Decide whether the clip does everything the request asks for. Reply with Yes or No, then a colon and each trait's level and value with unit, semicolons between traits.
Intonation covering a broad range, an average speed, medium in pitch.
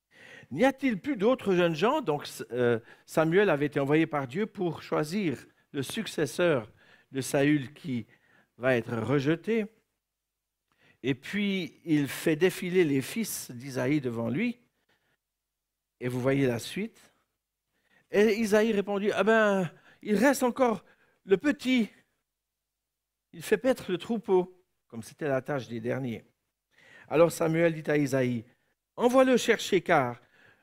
No: wide, 8.0 semitones; slow, 135 wpm; medium, 170 Hz